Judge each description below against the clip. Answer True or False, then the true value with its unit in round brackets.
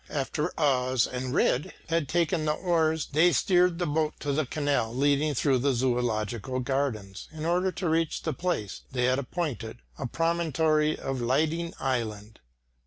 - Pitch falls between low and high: True (145 Hz)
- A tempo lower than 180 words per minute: True (160 wpm)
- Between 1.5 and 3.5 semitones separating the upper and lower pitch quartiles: False (4.3 semitones)